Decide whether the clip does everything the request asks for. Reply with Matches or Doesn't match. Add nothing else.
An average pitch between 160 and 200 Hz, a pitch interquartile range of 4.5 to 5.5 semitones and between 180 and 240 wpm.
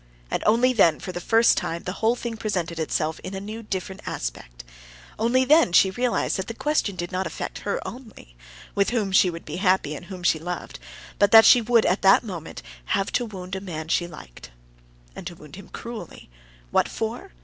Matches